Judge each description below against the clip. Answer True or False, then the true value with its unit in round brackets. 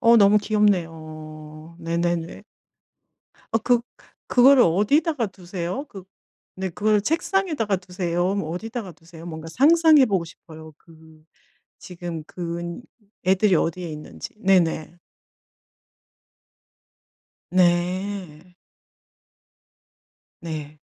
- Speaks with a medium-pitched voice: True (180 Hz)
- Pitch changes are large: False (4.3 semitones)